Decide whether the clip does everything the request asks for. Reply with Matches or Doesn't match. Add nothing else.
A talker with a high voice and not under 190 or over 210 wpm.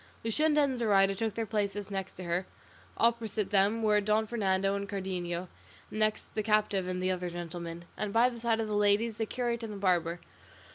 Matches